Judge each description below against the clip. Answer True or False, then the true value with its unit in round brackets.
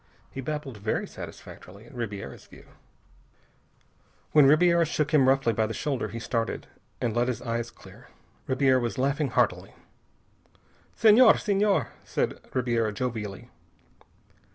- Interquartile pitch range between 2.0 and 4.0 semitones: False (4.6 semitones)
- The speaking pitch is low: True (130 Hz)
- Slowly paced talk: True (130 wpm)